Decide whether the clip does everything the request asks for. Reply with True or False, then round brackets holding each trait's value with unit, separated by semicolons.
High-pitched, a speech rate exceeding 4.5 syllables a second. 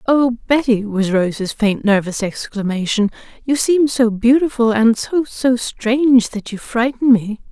False (235 Hz; 4.2 syllables/s)